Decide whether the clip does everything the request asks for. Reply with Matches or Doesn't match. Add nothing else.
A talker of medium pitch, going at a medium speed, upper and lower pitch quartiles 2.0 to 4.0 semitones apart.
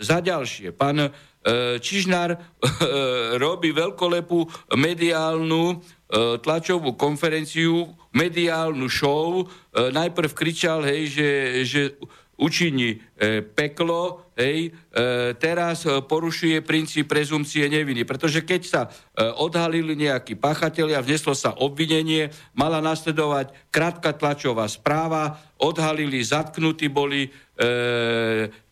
Doesn't match